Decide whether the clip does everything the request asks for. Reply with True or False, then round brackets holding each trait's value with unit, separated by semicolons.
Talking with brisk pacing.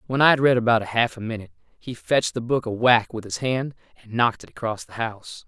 True (250 wpm)